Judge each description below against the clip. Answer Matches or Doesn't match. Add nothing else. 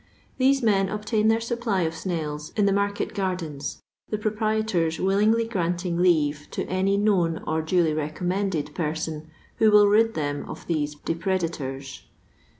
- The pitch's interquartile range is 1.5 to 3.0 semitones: Doesn't match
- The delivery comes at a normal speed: Matches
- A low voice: Doesn't match